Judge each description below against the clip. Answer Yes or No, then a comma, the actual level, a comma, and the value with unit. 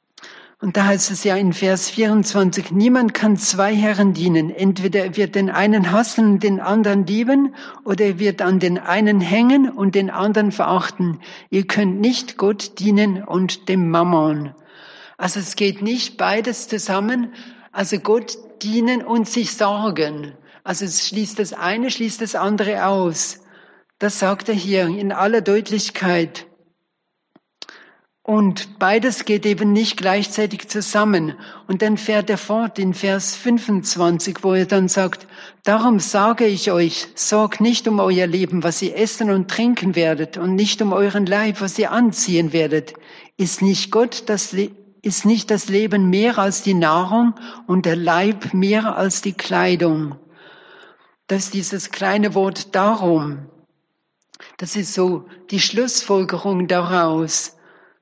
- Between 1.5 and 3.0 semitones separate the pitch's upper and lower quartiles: Yes, average, 2.7 semitones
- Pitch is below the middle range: No, high, 200 Hz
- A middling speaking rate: Yes, average, 150 wpm